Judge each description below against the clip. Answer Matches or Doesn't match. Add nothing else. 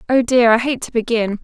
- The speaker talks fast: Matches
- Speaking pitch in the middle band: Doesn't match